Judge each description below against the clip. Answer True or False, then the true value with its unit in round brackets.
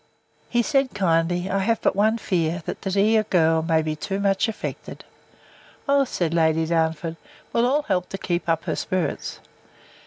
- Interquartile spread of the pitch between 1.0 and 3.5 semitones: False (4.7 semitones)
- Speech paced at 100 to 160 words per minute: False (175 wpm)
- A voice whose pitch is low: False (185 Hz)